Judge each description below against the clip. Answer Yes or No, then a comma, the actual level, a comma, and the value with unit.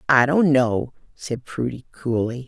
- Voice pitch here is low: Yes, low, 130 Hz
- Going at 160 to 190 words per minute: No, average, 145 wpm